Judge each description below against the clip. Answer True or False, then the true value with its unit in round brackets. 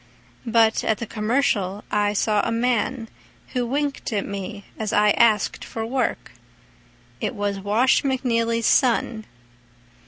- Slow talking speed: True (130 wpm)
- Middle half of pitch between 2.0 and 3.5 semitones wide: True (2.7 semitones)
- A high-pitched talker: True (225 Hz)